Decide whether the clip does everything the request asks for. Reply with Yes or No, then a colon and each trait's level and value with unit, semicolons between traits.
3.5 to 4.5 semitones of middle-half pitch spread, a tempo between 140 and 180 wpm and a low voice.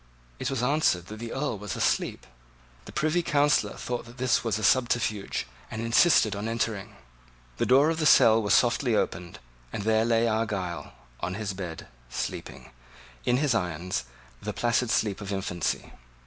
Yes: average, 3.9 semitones; average, 165 wpm; low, 115 Hz